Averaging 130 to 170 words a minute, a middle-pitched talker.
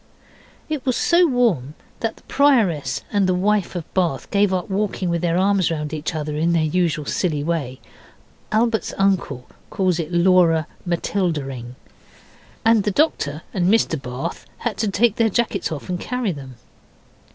Yes: average, 165 wpm; medium, 180 Hz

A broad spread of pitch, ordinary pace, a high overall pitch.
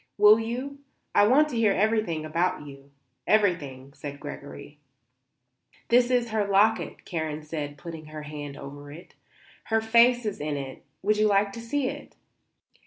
Yes: wide, 7.1 semitones; average, 160 wpm; high, 195 Hz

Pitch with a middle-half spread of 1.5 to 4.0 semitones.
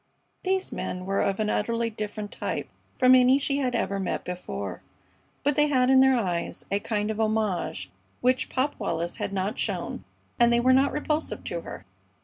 No: average, 4.6 semitones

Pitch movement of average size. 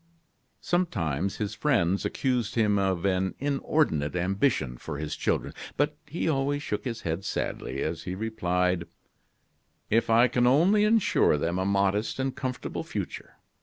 No: wide, 6.9 semitones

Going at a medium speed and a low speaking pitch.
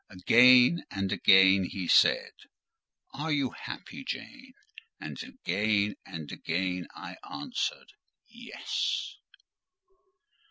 No: slow, 90 wpm; low, 105 Hz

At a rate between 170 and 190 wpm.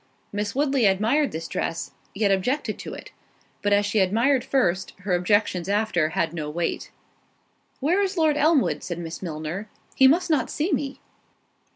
No: average, 160 wpm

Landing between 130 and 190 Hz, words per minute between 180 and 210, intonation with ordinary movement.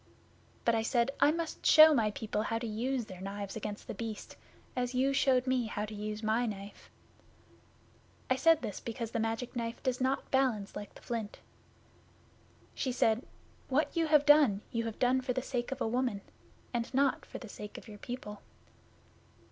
No: high, 235 Hz; average, 190 wpm; average, 3.4 semitones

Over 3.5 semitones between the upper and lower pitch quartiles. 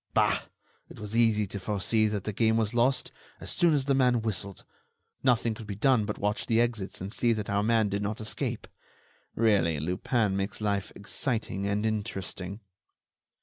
No: narrow, 2.5 semitones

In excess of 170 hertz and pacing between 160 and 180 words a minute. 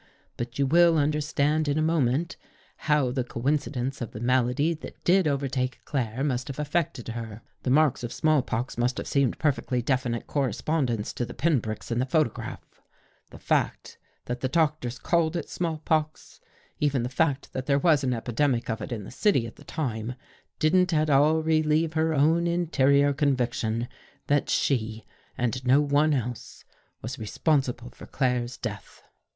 No: low, 135 Hz; average, 170 wpm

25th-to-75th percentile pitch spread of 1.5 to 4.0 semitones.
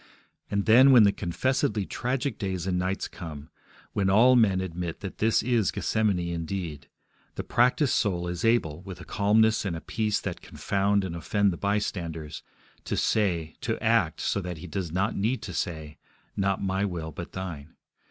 Yes: average, 3.7 semitones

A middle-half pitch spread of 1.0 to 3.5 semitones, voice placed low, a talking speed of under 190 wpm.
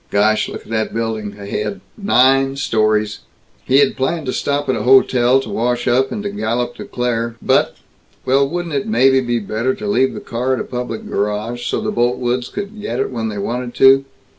No: average, 3.1 semitones; low, 125 Hz; fast, 205 wpm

